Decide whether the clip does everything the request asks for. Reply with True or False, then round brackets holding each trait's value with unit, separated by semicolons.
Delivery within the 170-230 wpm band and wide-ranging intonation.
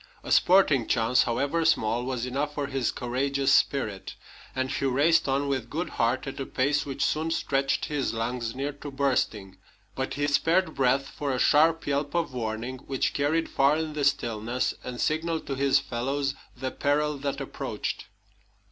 False (175 wpm; 2.5 semitones)